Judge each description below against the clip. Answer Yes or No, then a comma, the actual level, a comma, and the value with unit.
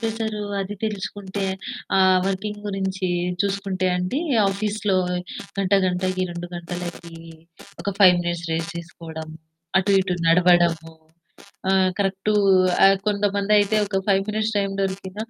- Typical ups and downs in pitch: No, narrow, 2.2 semitones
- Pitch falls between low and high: No, high, 195 Hz